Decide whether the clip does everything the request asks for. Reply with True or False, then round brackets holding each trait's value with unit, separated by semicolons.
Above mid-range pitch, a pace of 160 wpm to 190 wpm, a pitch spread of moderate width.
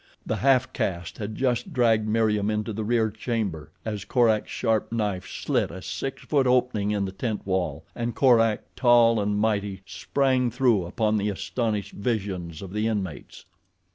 False (110 Hz; 165 wpm; 3.0 semitones)